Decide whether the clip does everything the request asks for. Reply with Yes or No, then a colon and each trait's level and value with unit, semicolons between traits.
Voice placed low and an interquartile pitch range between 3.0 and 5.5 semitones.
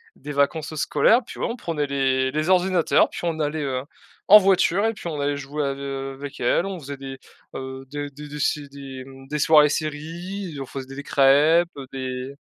No: medium, 145 Hz; average, 3.3 semitones